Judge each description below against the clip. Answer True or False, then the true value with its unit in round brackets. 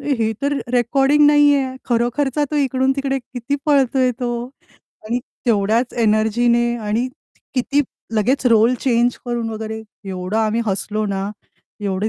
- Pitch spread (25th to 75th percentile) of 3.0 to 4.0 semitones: True (3.7 semitones)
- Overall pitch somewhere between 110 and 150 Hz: False (240 Hz)